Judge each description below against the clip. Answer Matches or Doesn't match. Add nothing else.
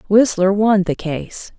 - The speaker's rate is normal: Matches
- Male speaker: Doesn't match